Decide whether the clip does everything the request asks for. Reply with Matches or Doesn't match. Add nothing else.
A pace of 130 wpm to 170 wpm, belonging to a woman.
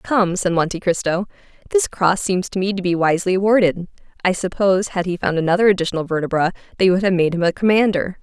Doesn't match